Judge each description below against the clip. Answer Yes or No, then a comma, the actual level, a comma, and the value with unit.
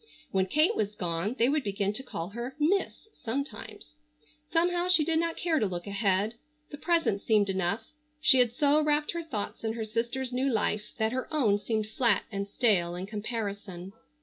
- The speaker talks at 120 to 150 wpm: No, average, 185 wpm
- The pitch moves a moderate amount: No, wide, 6.3 semitones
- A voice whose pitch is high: Yes, high, 225 Hz